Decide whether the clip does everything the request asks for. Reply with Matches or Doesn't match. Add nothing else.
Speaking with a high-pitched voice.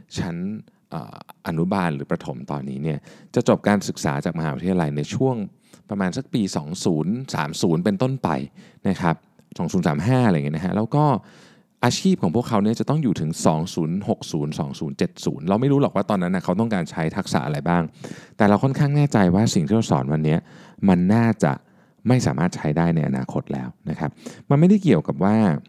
Doesn't match